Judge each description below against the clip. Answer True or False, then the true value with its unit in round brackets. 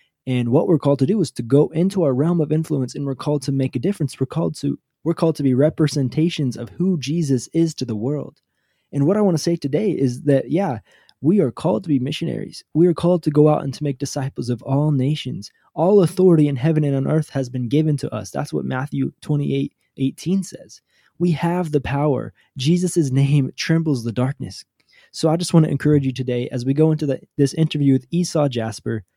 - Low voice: False (145 Hz)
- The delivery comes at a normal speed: False (225 wpm)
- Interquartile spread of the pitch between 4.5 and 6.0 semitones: False (3.4 semitones)